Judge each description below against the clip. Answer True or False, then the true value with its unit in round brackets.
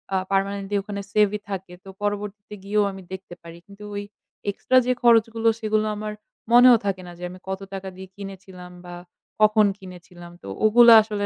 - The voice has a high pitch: True (200 Hz)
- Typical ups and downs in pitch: False (2.0 semitones)